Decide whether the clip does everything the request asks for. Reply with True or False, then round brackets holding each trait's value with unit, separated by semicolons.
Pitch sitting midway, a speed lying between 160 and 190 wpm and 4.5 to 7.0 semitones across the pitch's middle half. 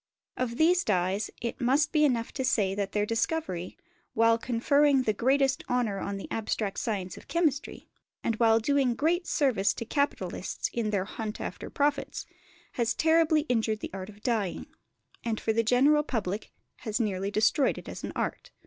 False (230 Hz; 175 wpm; 5.0 semitones)